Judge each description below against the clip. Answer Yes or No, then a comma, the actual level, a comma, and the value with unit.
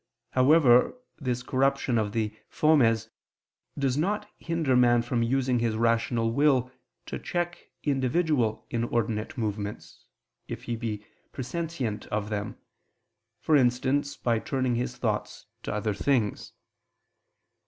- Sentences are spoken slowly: Yes, slow, 120 wpm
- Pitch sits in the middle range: No, low, 125 Hz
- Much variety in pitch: No, average, 3.5 semitones